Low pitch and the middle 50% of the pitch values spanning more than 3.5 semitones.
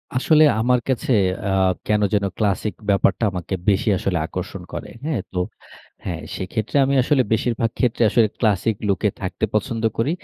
Yes: low, 110 Hz; average, 3.9 semitones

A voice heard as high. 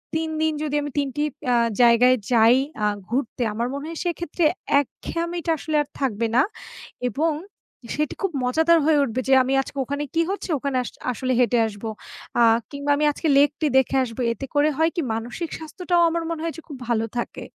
Yes: very high, 285 Hz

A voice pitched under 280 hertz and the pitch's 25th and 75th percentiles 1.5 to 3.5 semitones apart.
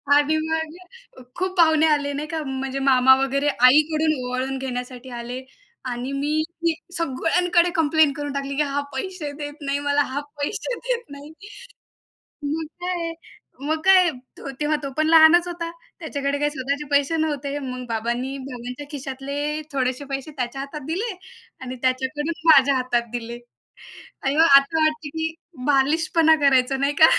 No: very high, 285 Hz; average, 3.1 semitones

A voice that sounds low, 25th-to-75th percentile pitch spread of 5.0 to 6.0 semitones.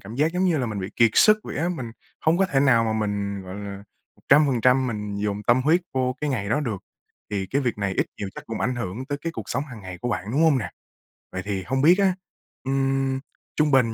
Yes: low, 125 Hz; wide, 5.5 semitones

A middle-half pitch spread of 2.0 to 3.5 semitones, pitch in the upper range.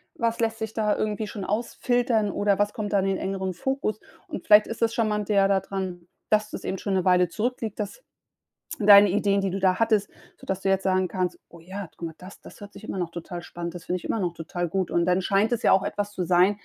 Yes: narrow, 2.6 semitones; high, 195 Hz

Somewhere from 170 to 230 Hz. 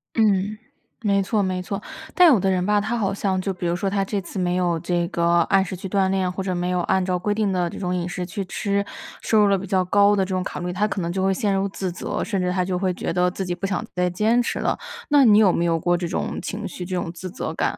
Yes: high, 190 Hz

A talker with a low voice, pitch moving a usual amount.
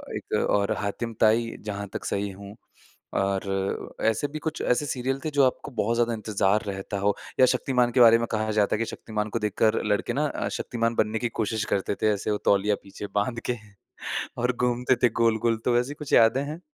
Yes: low, 115 Hz; average, 3.1 semitones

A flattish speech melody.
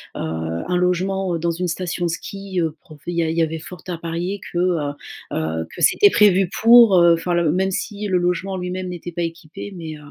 Yes: narrow, 2.2 semitones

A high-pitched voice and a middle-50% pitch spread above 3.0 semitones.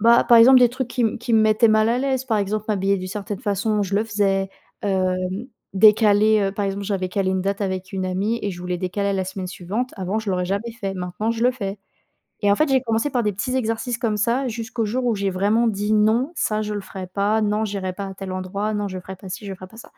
No: high, 205 Hz; average, 2.7 semitones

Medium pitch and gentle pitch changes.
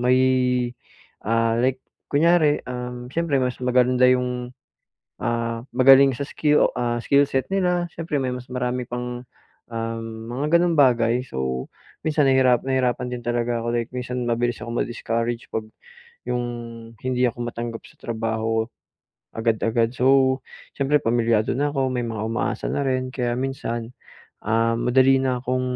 No: low, 125 Hz; narrow, 2.0 semitones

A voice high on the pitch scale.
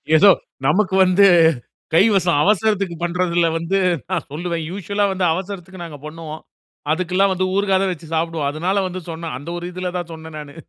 No: medium, 175 Hz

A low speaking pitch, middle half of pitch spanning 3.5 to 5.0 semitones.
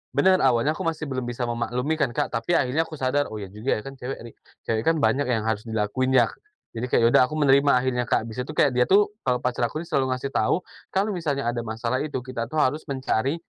Yes: low, 130 Hz; average, 3.8 semitones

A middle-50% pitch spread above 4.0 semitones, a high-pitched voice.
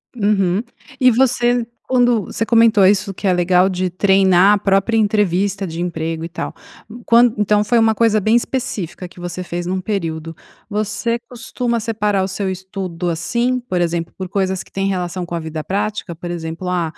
No: average, 3.7 semitones; high, 195 Hz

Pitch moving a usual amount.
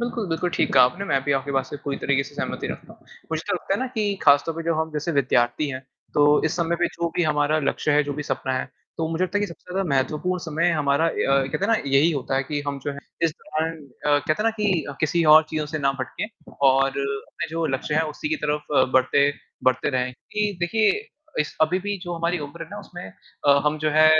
Yes: average, 3.5 semitones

